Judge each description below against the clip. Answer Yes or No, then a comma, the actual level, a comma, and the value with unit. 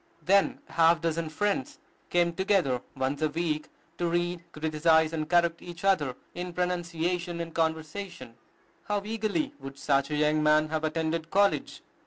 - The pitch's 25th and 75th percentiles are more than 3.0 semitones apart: No, narrow, 2.4 semitones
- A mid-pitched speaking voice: Yes, medium, 165 Hz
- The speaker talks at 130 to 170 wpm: Yes, average, 155 wpm